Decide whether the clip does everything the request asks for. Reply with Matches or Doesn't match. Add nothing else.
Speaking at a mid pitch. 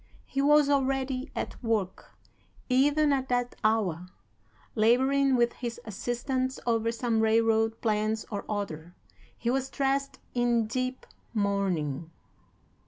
Doesn't match